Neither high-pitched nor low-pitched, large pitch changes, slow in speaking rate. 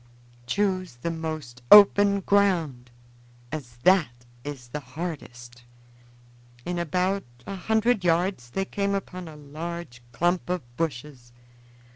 Yes: medium, 165 Hz; wide, 6.5 semitones; slow, 115 wpm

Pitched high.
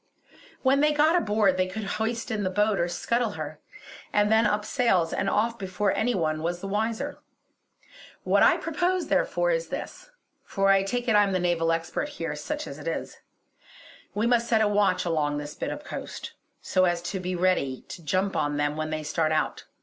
Yes: high, 200 Hz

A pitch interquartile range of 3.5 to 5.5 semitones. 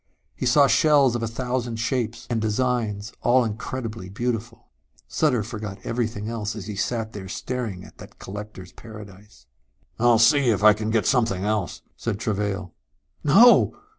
No: average, 2.8 semitones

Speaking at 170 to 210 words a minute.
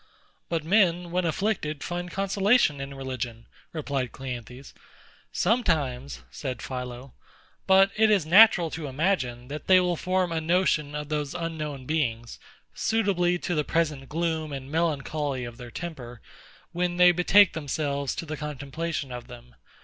No: average, 145 wpm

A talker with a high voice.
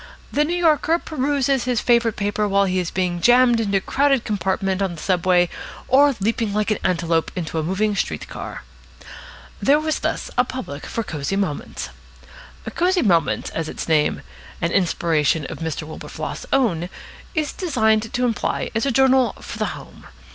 Yes: high, 210 Hz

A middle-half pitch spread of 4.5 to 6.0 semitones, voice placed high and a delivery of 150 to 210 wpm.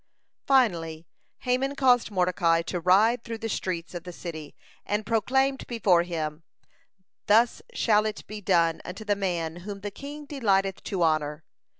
Yes: average, 5.1 semitones; high, 195 Hz; average, 160 wpm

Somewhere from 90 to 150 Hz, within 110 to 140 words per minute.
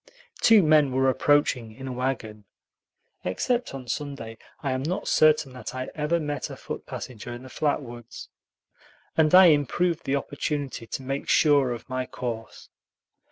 No: low, 135 Hz; average, 160 wpm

